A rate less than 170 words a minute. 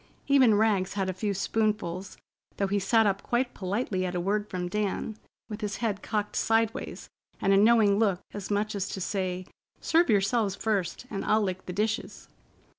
No: average, 185 wpm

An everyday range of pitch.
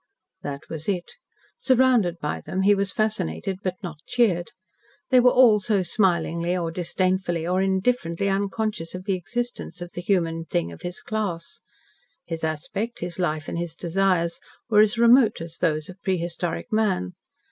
Yes: average, 3.8 semitones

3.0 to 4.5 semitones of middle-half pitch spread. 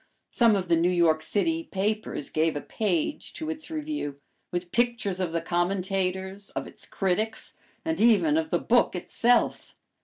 No: average, 5.3 semitones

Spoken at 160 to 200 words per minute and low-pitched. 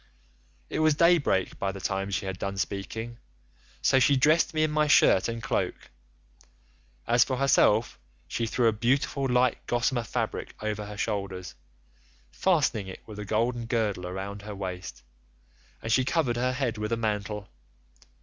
Yes: average, 165 wpm; low, 115 Hz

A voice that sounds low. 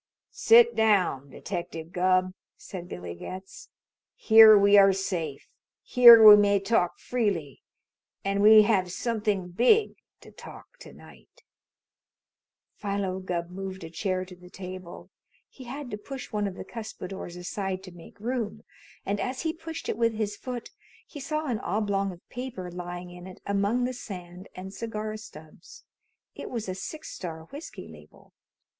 No: high, 200 Hz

